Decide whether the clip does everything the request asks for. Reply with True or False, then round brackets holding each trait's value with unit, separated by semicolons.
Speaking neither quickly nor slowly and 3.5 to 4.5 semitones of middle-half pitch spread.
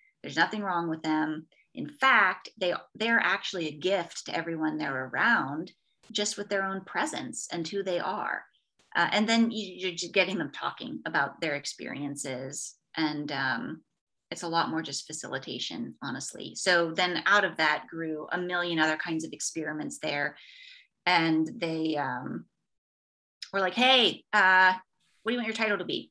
True (170 wpm; 4.1 semitones)